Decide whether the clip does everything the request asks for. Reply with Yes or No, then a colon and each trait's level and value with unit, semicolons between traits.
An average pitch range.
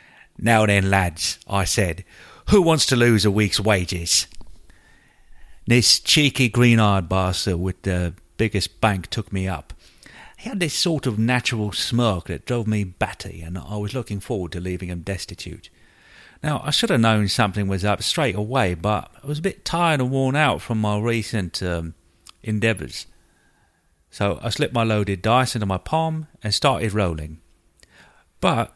Yes: average, 4.8 semitones